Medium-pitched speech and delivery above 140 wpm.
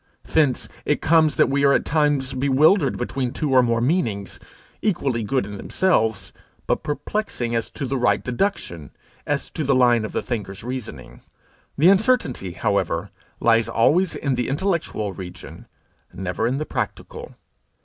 No: low, 130 Hz; average, 155 wpm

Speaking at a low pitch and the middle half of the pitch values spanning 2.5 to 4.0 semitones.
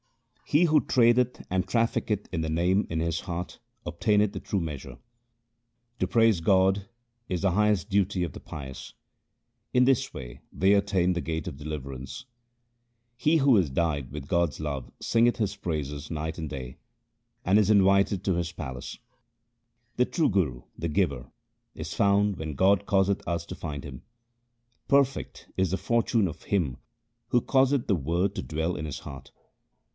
No: very low, 90 Hz; average, 5.1 semitones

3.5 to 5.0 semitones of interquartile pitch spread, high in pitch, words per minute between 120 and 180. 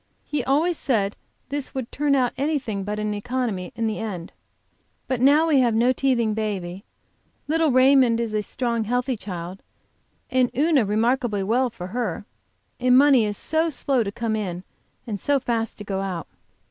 Yes: average, 4.2 semitones; high, 235 Hz; average, 170 wpm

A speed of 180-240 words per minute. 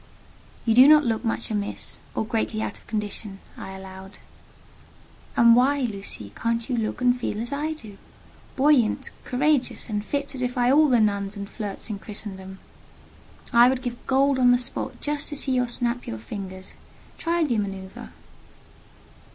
No: average, 165 wpm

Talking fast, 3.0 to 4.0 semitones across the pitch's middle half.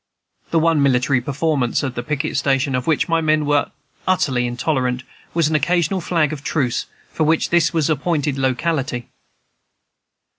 No: average, 160 wpm; average, 3.7 semitones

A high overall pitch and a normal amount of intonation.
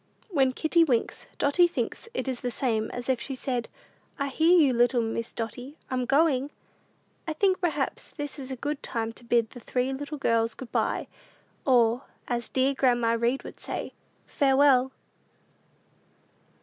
Yes: very high, 260 Hz; average, 3.1 semitones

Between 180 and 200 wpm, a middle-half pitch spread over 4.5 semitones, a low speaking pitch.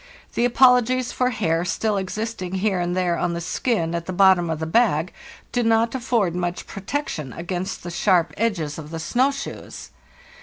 No: average, 185 wpm; average, 5.2 semitones; medium, 185 Hz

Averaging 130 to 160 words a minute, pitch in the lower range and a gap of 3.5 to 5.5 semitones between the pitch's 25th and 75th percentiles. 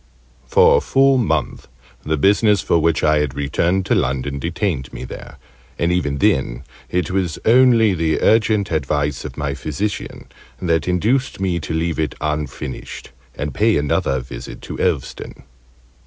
Yes: average, 155 wpm; very low, 80 Hz; average, 5.2 semitones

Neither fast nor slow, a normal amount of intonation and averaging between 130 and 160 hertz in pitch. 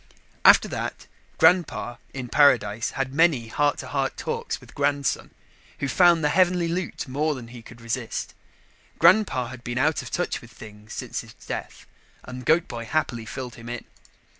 Yes: average, 170 wpm; average, 4.9 semitones; low, 135 Hz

